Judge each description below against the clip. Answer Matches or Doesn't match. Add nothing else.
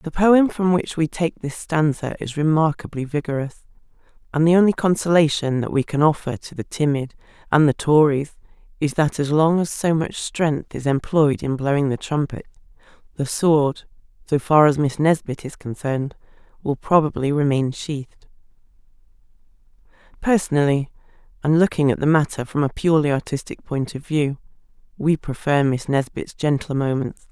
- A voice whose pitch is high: Doesn't match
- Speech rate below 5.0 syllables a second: Doesn't match